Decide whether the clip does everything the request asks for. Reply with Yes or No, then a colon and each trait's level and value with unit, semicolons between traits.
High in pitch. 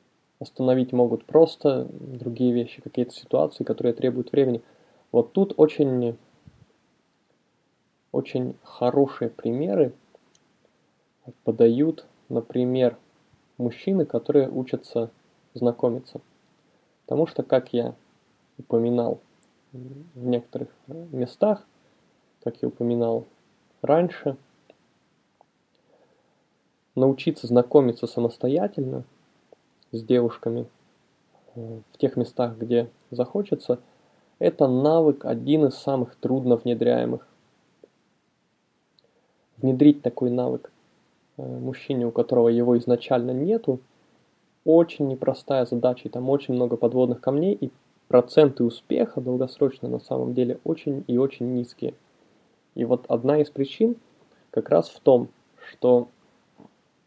No: low, 125 Hz